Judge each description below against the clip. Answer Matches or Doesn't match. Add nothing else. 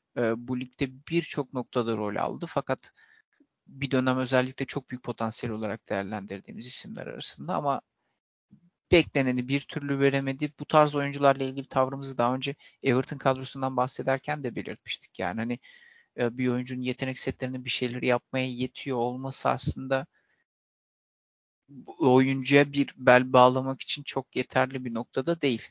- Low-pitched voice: Matches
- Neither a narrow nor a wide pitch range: Doesn't match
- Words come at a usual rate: Matches